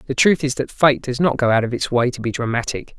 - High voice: No, low, 130 Hz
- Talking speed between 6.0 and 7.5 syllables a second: Yes, 6.1 syllables/s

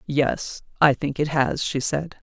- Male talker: No, female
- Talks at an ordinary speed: Yes, average, 180 wpm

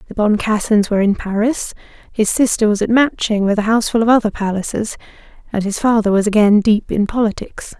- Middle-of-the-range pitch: No, high, 215 Hz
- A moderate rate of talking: Yes, average, 185 wpm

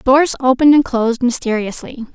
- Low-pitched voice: No, very high, 255 Hz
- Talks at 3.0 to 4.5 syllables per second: No, 5.7 syllables/s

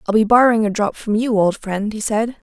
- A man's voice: No, female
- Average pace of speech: No, fast, 260 wpm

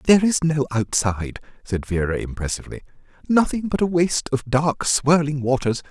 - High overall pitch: No, medium, 140 Hz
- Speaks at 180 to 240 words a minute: No, average, 150 wpm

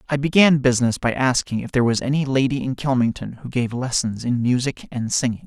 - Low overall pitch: Yes, low, 130 Hz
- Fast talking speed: Yes, fast, 210 wpm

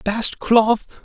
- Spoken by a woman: No, male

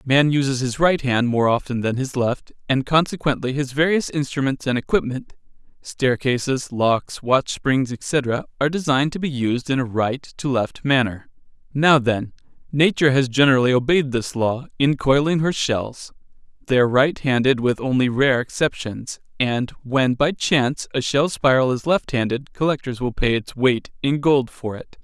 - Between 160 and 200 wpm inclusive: Yes, average, 170 wpm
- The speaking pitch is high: No, low, 135 Hz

